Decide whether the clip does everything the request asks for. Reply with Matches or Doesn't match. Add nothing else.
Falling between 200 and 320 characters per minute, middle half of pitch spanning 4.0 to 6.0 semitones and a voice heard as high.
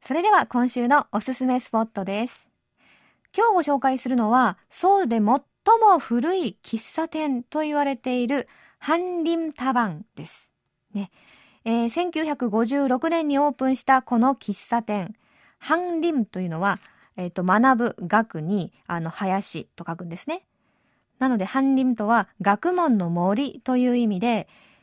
Matches